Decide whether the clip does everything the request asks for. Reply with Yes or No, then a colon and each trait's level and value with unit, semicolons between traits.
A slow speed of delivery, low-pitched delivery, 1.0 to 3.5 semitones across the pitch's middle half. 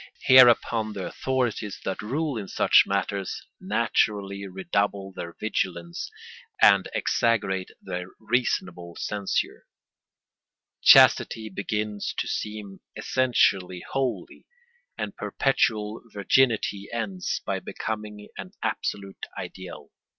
Yes: slow, 95 wpm; low, 105 Hz; average, 2.7 semitones